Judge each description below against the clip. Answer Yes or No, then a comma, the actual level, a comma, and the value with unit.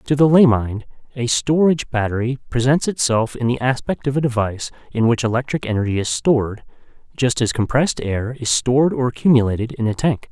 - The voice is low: Yes, low, 125 Hz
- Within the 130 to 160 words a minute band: No, average, 185 wpm